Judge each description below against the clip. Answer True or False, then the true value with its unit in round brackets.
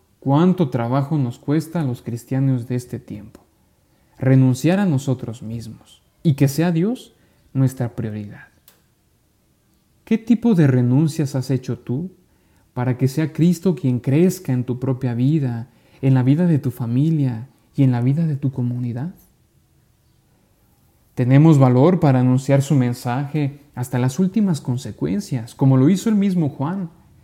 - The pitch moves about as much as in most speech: True (4.2 semitones)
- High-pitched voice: False (135 Hz)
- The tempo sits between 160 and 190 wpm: False (145 wpm)